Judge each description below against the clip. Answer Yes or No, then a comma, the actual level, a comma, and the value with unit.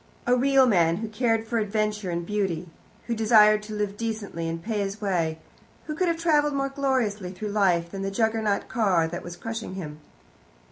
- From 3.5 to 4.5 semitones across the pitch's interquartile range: Yes, average, 3.9 semitones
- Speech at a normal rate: Yes, average, 190 wpm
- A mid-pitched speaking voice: No, high, 210 Hz